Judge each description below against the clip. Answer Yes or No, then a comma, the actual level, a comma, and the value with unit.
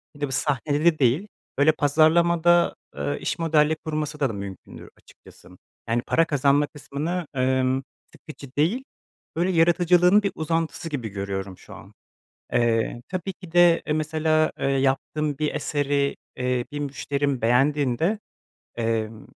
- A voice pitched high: No, medium, 145 Hz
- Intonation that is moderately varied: Yes, average, 4.0 semitones